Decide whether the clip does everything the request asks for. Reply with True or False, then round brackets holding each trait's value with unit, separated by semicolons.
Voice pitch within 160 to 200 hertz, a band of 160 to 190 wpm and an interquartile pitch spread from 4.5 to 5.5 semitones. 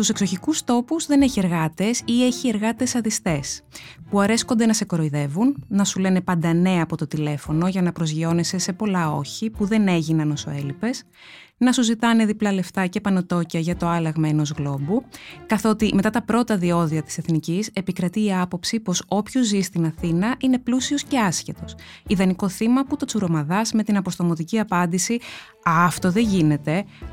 True (190 Hz; 170 wpm; 5.1 semitones)